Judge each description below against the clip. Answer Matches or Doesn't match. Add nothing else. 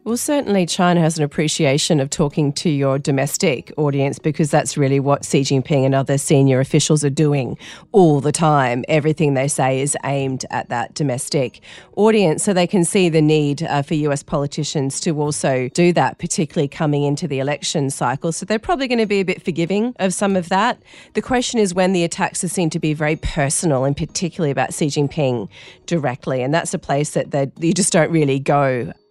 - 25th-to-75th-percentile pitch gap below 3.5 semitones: Doesn't match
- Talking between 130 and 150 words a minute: Doesn't match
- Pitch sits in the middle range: Matches